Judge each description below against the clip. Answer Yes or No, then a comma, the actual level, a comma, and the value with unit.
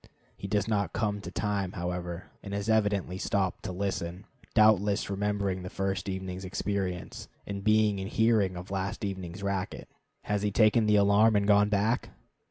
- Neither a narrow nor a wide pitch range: No, narrow, 1.7 semitones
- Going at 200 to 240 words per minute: No, average, 170 wpm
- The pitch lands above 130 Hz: No, low, 100 Hz